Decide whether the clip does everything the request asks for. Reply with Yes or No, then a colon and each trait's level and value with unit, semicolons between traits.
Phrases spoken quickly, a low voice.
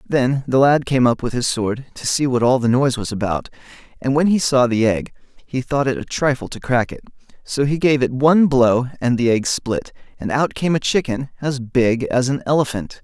Yes: fast, 230 wpm; low, 130 Hz